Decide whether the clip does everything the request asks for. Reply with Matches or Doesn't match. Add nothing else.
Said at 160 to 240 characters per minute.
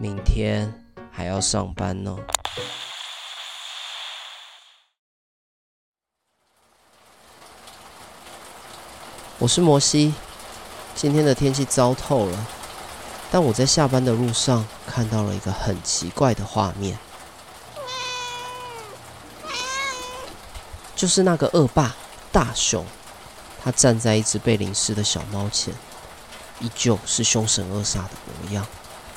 Doesn't match